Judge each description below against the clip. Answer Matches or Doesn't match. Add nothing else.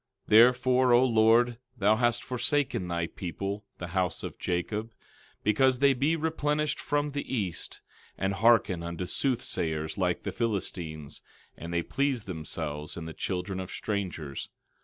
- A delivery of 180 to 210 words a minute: Doesn't match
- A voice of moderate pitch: Doesn't match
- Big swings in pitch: Matches